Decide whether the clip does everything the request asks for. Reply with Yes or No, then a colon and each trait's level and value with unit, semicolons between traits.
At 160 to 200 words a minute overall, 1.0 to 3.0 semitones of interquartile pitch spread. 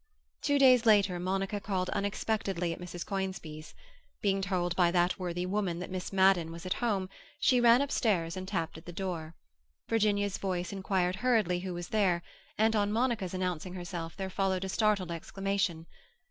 Yes: average, 170 wpm; narrow, 2.4 semitones